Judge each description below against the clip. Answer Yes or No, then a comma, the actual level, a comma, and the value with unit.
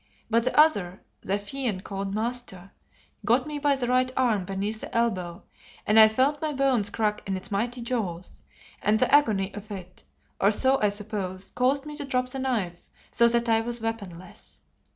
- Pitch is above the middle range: Yes, high, 225 Hz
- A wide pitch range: No, average, 4.3 semitones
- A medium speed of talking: Yes, average, 185 wpm